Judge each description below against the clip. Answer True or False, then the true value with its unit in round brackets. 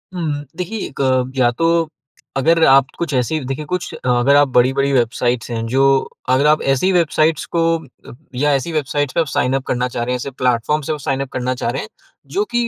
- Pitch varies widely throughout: False (3.4 semitones)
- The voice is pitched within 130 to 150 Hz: True (135 Hz)